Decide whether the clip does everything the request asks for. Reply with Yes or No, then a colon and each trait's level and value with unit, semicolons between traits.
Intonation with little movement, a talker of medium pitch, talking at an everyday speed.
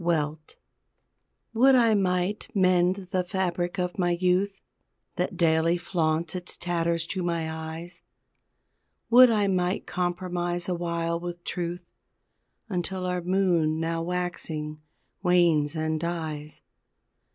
No: narrow, 1.7 semitones; medium, 175 Hz; slow, 115 wpm